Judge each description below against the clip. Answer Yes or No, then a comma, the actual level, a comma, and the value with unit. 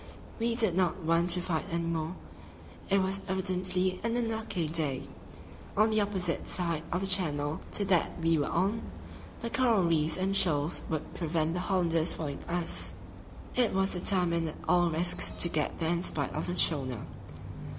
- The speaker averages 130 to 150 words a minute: No, average, 170 wpm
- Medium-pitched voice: Yes, medium, 175 Hz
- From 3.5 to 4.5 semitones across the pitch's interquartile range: No, average, 2.8 semitones